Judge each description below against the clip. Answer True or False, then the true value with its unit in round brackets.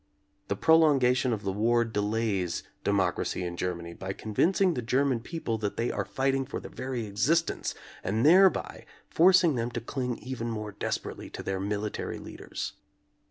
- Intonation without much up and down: False (4.9 semitones)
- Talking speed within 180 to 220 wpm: False (165 wpm)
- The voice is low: True (115 Hz)